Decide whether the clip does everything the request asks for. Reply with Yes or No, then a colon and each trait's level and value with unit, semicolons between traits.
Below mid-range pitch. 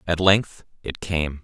Yes: very low, 85 Hz